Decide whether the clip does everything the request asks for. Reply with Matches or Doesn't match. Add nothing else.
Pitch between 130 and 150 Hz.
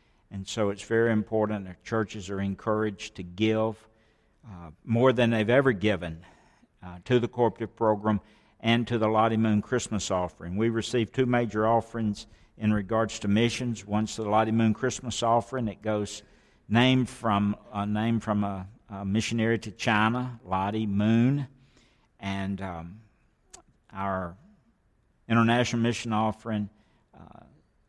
Doesn't match